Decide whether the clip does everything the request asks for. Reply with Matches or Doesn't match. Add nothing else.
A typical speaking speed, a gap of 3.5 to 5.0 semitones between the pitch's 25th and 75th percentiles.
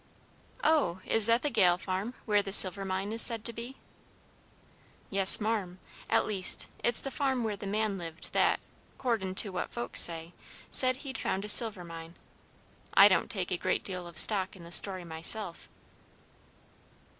Matches